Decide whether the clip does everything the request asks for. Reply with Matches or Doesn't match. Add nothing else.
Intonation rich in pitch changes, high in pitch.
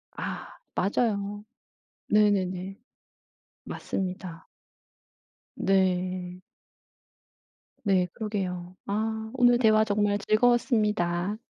Doesn't match